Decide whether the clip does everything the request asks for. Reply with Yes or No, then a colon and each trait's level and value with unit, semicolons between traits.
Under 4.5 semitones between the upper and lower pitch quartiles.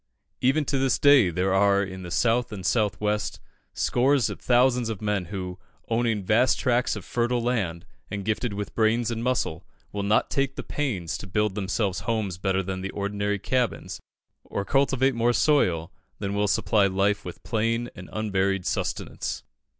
Yes: average, 3.8 semitones